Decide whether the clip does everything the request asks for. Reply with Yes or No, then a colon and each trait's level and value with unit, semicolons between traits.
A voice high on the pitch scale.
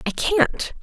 Yes: very high, 325 Hz